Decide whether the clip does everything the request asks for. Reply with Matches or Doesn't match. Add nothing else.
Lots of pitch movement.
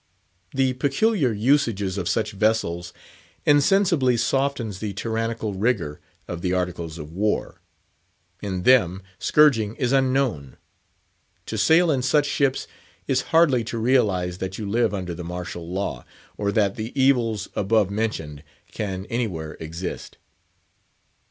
Matches